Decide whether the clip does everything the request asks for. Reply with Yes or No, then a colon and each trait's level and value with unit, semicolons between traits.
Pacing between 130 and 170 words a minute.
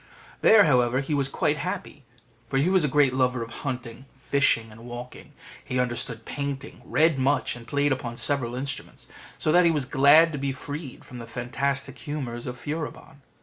No: average, 185 wpm